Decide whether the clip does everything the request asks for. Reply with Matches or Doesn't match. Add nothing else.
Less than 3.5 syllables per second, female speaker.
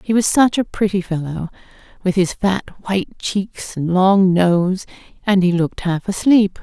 Doesn't match